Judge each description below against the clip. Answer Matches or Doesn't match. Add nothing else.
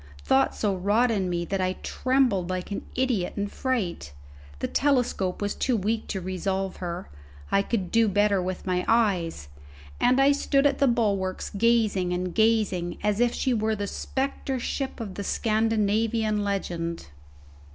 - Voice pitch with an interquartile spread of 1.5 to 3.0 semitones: Doesn't match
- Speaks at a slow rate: Doesn't match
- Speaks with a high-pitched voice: Matches